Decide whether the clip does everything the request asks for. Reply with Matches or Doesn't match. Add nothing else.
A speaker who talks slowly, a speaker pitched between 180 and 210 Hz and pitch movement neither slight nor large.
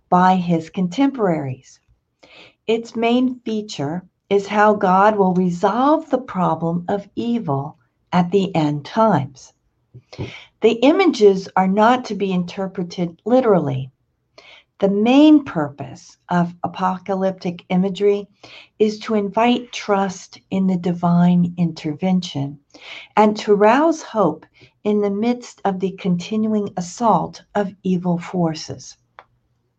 Matches